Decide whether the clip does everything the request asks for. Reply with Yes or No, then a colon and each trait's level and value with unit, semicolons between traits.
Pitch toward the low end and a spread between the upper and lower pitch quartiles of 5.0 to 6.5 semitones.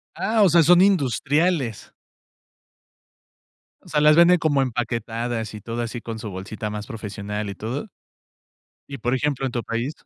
Yes: low, 120 Hz; average, 5.3 semitones